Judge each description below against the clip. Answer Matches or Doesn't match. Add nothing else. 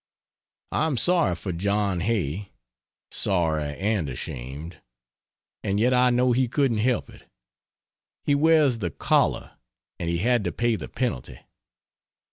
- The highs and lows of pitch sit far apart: Matches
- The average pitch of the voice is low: Matches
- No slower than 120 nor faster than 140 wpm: Matches